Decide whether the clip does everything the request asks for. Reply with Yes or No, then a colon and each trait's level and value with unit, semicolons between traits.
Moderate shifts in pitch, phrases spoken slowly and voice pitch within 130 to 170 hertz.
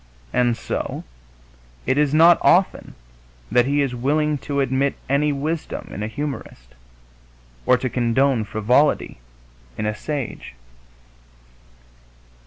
Yes: average, 3.6 semitones; slow, 115 wpm; low, 135 Hz